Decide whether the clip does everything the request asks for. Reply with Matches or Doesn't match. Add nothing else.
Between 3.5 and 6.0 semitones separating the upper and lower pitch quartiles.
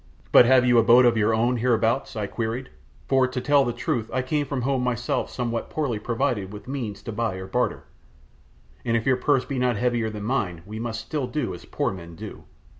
Doesn't match